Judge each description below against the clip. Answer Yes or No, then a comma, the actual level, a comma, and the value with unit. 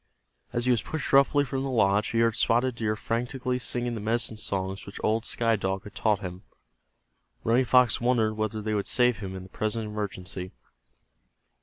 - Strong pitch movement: No, average, 2.9 semitones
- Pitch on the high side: No, low, 110 Hz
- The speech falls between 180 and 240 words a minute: Yes, average, 185 wpm